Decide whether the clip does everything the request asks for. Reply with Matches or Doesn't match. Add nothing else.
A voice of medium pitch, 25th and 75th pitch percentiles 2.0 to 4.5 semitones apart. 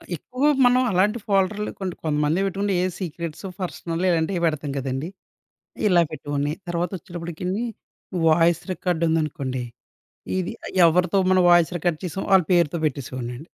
Matches